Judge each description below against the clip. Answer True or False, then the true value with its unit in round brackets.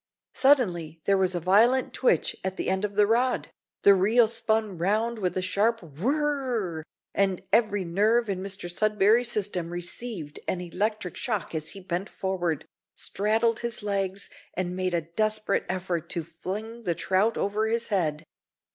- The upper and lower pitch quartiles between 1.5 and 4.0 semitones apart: True (3.7 semitones)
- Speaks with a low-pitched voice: False (200 Hz)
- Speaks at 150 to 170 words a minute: True (165 wpm)